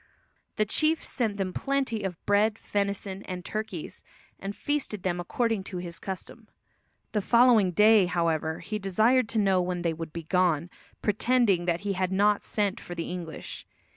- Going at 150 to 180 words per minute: Yes, average, 170 wpm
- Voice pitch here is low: No, high, 195 Hz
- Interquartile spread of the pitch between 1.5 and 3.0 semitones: No, average, 3.4 semitones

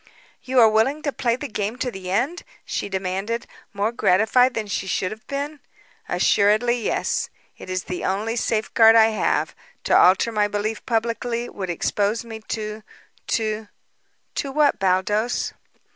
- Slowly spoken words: No, average, 160 wpm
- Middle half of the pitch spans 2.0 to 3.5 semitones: Yes, average, 2.9 semitones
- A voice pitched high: Yes, high, 220 Hz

